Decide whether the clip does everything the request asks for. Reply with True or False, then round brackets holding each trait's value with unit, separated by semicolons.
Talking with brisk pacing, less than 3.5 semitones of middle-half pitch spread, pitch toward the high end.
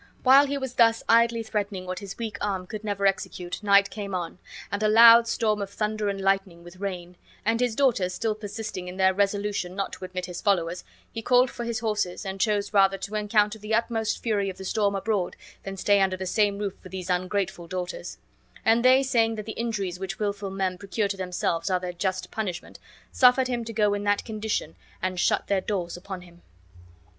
True (210 wpm; 2.9 semitones; 200 Hz)